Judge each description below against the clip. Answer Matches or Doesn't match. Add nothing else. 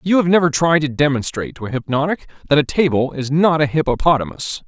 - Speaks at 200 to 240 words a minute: Matches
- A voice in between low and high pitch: Matches